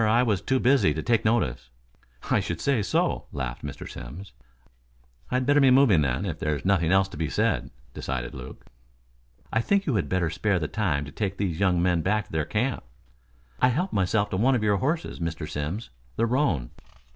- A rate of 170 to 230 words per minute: Yes, average, 200 wpm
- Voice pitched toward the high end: No, low, 100 Hz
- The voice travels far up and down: Yes, wide, 7.0 semitones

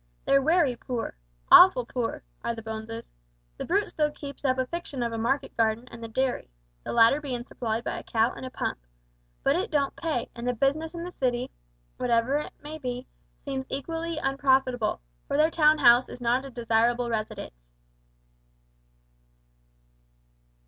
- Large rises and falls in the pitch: No, average, 3.7 semitones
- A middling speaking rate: Yes, average, 170 wpm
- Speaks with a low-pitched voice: No, very high, 255 Hz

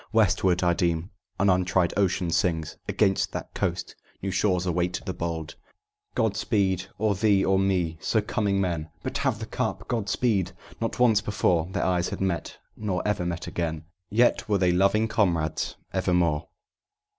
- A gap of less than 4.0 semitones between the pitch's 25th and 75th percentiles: Yes, average, 2.9 semitones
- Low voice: Yes, very low, 95 Hz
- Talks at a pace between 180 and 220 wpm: No, average, 165 wpm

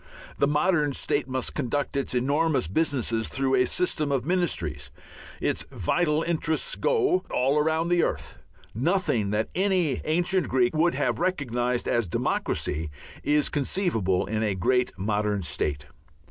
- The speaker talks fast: No, average, 140 wpm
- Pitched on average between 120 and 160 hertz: Yes, medium, 140 Hz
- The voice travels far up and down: Yes, wide, 6.4 semitones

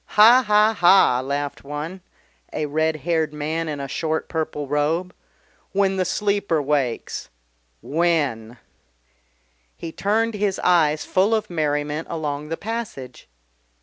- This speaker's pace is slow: Yes, slow, 125 wpm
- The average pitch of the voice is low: No, medium, 160 Hz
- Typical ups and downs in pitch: Yes, average, 4.6 semitones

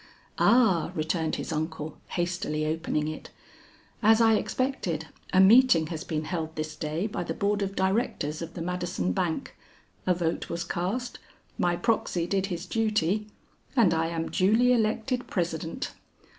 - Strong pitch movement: No, average, 4.8 semitones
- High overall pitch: No, medium, 175 Hz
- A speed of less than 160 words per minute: Yes, average, 150 wpm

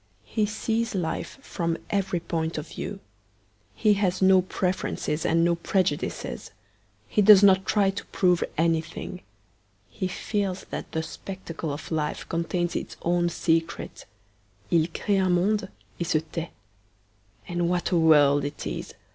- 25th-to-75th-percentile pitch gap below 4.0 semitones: Yes, average, 2.7 semitones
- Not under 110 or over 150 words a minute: Yes, average, 145 wpm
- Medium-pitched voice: Yes, medium, 175 Hz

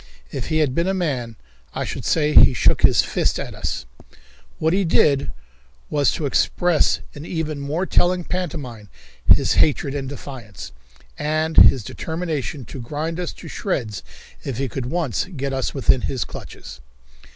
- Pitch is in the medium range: Yes, medium, 145 Hz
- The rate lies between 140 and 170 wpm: Yes, average, 160 wpm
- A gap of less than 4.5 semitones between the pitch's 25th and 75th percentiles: Yes, average, 3.8 semitones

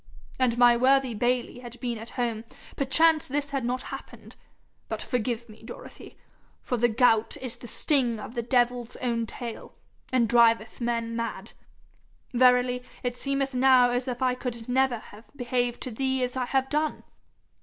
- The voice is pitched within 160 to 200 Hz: No, high, 245 Hz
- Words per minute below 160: No, average, 165 wpm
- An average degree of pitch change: No, narrow, 1.7 semitones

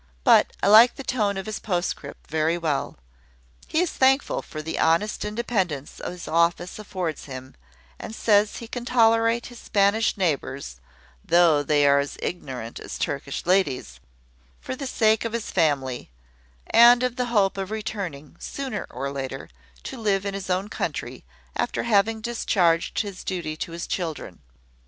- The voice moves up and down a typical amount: No, wide, 6.3 semitones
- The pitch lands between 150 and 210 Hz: Yes, high, 190 Hz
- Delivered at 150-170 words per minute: Yes, average, 160 wpm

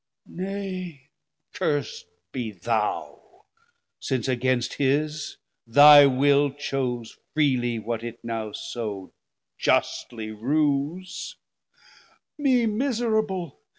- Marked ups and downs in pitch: Yes, wide, 6.1 semitones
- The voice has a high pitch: No, medium, 140 Hz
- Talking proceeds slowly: Yes, slow, 85 wpm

